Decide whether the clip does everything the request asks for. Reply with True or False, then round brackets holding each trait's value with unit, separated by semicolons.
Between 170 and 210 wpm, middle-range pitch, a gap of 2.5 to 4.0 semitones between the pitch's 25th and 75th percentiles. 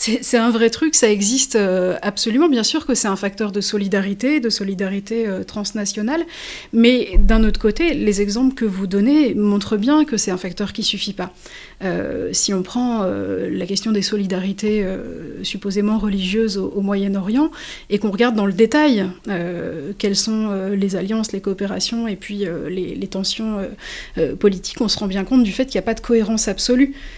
False (205 wpm; 210 Hz; 2.8 semitones)